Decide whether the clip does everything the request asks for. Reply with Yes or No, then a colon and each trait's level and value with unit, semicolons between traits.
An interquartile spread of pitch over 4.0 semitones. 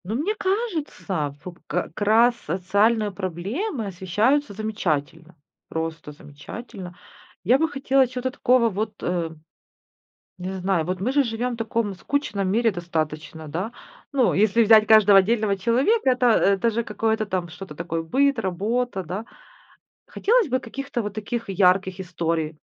Yes: average, 5.1 semitones